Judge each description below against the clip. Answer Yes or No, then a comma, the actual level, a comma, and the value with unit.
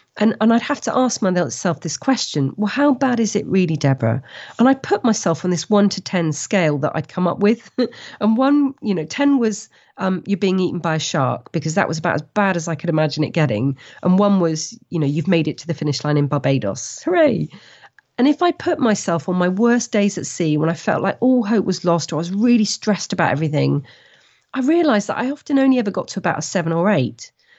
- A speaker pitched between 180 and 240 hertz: Yes, high, 190 Hz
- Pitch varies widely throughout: Yes, wide, 5.9 semitones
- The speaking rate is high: Yes, fast, 240 wpm